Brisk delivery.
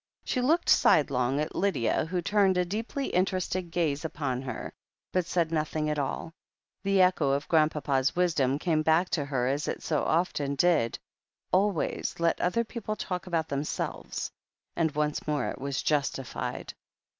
No: average, 160 wpm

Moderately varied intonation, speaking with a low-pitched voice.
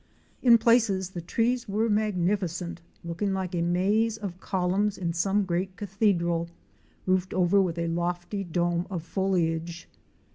No: average, 3.0 semitones; medium, 185 Hz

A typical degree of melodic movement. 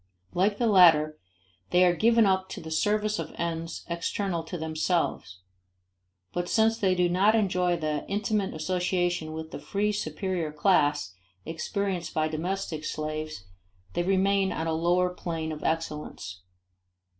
Yes: average, 3.6 semitones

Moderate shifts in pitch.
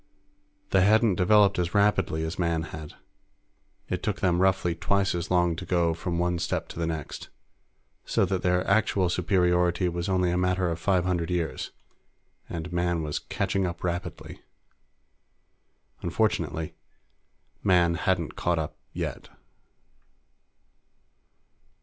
No: narrow, 1.6 semitones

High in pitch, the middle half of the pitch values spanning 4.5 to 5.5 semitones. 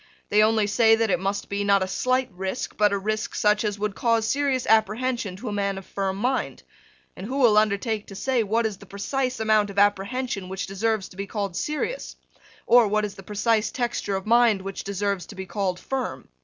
No: high, 210 Hz; average, 2.7 semitones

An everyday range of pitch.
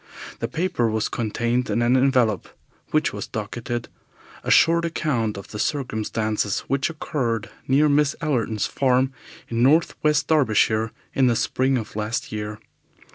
Yes: average, 4.4 semitones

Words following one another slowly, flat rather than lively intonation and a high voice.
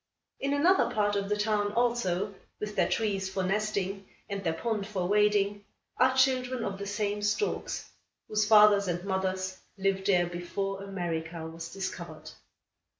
No: average, 150 wpm; narrow, 1.9 semitones; high, 200 Hz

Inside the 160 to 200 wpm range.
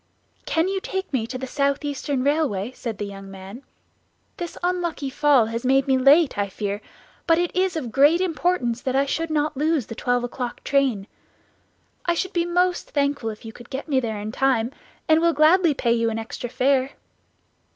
Yes: average, 195 wpm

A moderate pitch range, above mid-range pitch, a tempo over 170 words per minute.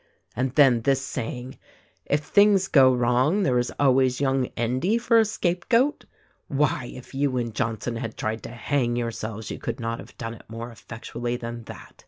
No: average, 3.4 semitones; low, 125 Hz; average, 190 wpm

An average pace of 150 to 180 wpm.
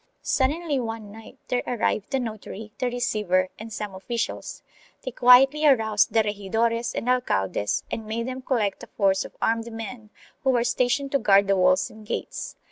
Yes: average, 175 wpm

